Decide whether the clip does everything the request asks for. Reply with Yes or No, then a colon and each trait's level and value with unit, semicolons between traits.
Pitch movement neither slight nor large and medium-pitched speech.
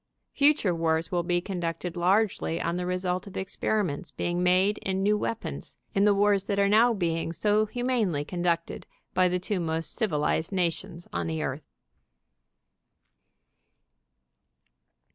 Yes: average, 3.3 semitones; medium, 180 Hz